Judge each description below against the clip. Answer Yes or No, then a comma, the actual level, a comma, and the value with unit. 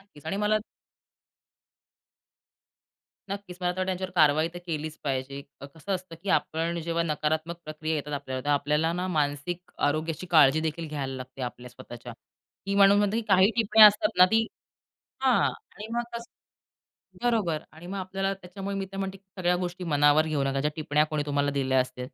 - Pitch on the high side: No, medium, 165 Hz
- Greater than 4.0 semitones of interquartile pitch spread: Yes, average, 4.7 semitones